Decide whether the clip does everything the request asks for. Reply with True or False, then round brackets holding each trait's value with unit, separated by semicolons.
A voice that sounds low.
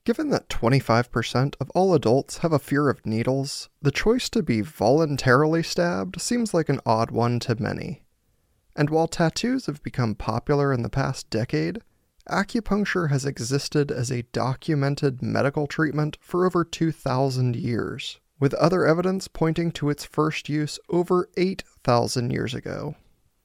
False (145 Hz)